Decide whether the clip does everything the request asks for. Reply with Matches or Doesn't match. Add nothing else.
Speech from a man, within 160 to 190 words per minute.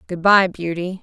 Doesn't match